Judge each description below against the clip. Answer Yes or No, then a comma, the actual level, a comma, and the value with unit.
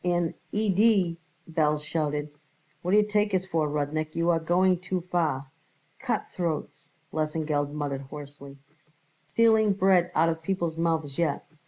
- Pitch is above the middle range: No, medium, 165 Hz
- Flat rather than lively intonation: No, average, 3.5 semitones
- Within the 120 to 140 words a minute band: Yes, slow, 135 wpm